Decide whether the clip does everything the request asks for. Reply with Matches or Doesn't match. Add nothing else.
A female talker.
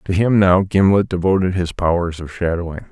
Doesn't match